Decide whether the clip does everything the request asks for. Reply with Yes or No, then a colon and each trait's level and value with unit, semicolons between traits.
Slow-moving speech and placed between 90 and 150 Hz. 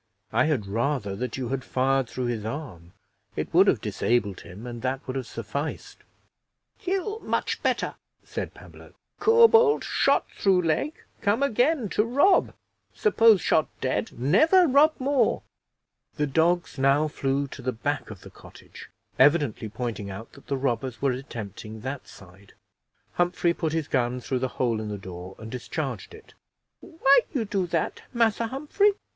No: average, 160 wpm; medium, 140 Hz